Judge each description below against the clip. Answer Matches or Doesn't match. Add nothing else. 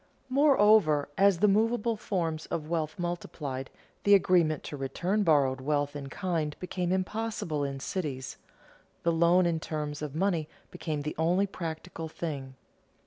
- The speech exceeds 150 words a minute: Doesn't match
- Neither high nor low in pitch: Matches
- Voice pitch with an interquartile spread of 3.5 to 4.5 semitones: Matches